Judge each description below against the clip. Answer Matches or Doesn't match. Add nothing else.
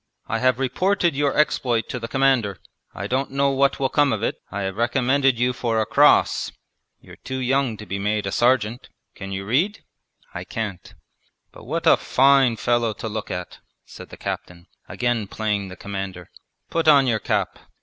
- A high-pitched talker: Doesn't match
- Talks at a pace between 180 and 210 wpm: Matches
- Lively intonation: Doesn't match